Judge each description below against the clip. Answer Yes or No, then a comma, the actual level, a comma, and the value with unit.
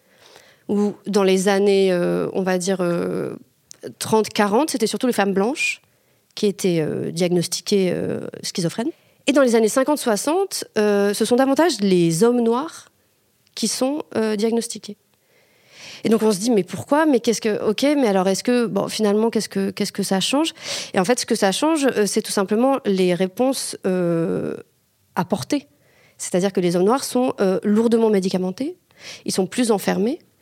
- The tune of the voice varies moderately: Yes, average, 4.5 semitones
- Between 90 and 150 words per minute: No, average, 170 wpm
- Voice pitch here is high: Yes, high, 215 Hz